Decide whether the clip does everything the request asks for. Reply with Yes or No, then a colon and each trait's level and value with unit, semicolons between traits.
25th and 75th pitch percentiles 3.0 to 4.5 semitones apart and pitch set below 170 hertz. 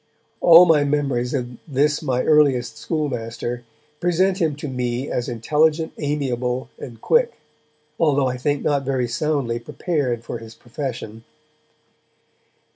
Yes: average, 3.7 semitones; low, 135 Hz